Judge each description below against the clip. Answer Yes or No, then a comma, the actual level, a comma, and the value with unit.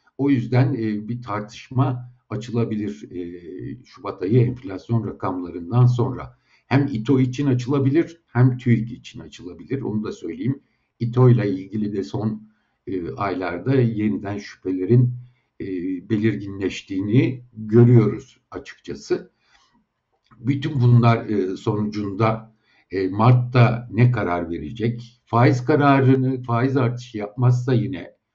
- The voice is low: Yes, low, 120 Hz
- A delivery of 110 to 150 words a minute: No, slow, 95 wpm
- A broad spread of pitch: No, average, 3.3 semitones